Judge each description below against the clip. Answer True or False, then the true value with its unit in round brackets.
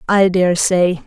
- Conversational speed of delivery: True (170 wpm)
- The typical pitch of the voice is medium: True (180 Hz)